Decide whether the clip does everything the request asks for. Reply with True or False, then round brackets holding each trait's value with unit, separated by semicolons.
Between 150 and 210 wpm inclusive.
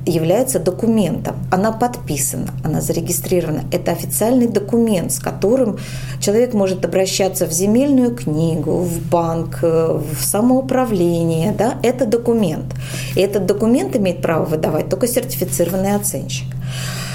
False (115 wpm)